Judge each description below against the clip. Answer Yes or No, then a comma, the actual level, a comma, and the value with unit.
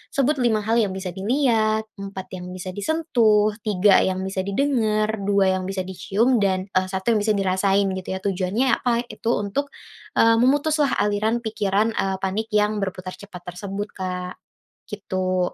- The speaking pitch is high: Yes, high, 205 Hz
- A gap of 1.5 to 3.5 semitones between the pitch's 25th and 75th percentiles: Yes, average, 2.8 semitones